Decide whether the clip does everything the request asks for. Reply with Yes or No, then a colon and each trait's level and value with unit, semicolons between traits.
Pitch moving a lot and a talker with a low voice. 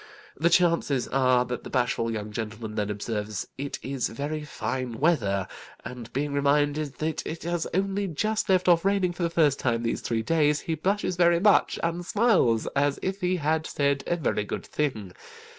No: wide, 6.1 semitones; medium, 145 Hz